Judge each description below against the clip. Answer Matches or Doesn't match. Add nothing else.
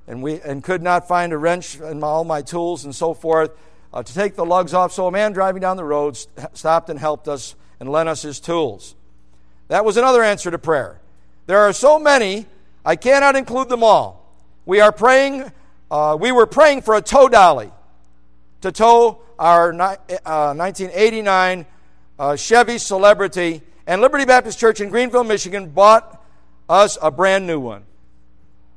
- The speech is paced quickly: Doesn't match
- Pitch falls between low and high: Matches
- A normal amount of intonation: Doesn't match